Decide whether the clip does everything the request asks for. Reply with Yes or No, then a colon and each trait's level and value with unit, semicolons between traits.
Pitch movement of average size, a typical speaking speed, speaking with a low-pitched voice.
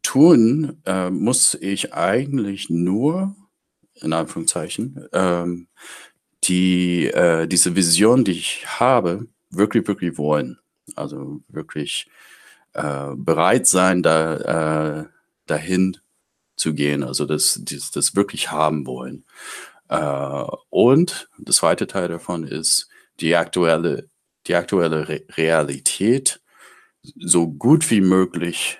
No: average, 3.4 semitones; slow, 110 wpm; very low, 85 Hz